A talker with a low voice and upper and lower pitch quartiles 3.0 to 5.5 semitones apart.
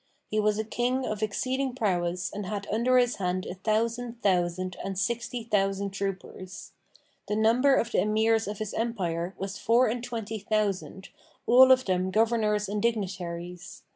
No: high, 210 Hz; average, 3.4 semitones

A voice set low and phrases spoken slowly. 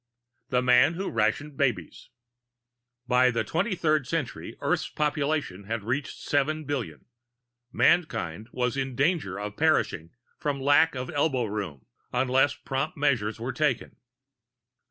Yes: low, 130 Hz; slow, 130 wpm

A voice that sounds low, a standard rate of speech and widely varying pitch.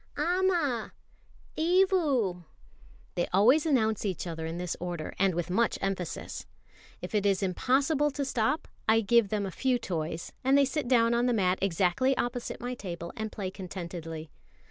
No: high, 220 Hz; average, 165 wpm; wide, 6.6 semitones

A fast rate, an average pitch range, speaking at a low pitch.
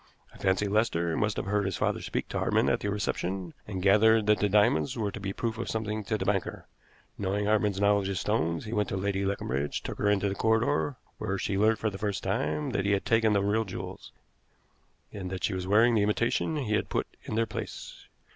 No: fast, 230 wpm; narrow, 2.0 semitones; low, 100 Hz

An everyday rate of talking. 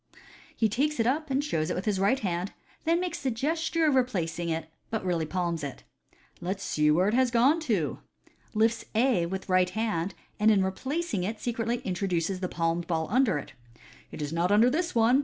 No: fast, 215 wpm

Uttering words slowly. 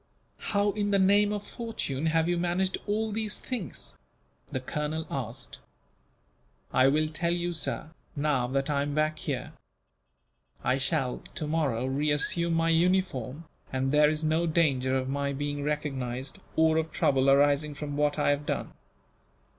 No: average, 155 wpm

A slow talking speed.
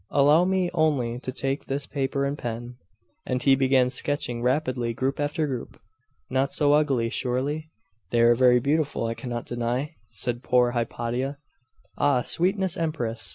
No: average, 155 wpm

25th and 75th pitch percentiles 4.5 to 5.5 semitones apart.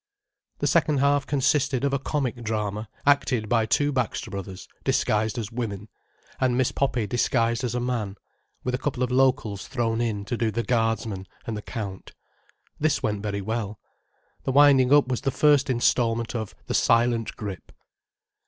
No: average, 3.3 semitones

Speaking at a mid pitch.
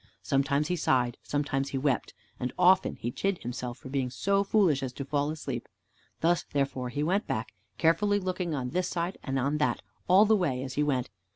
Yes: medium, 145 Hz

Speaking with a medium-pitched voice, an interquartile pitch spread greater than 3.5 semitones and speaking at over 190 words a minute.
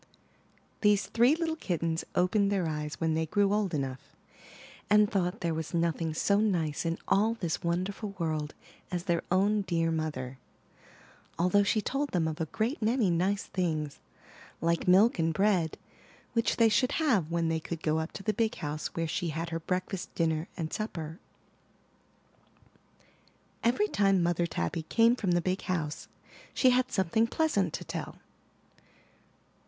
No: medium, 180 Hz; average, 4.4 semitones; average, 160 wpm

